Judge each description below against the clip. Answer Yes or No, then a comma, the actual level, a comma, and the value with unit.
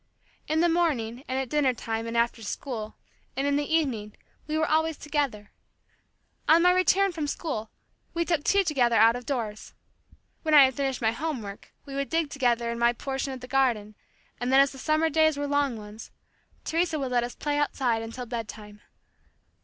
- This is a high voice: Yes, very high, 270 Hz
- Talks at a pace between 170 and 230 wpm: Yes, average, 200 wpm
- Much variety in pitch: No, average, 4.8 semitones